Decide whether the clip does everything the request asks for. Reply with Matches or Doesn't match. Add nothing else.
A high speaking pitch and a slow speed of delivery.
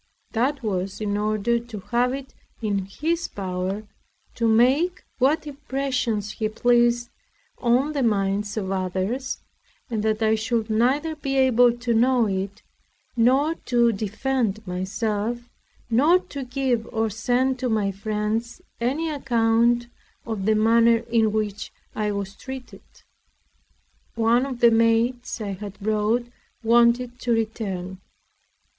Matches